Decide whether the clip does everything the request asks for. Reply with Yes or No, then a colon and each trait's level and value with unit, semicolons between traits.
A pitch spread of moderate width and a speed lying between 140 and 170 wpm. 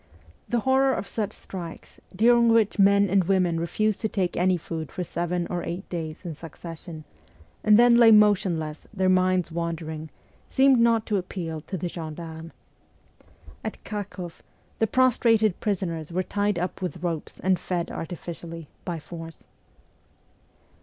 Yes: average, 3.9 semitones; average, 150 wpm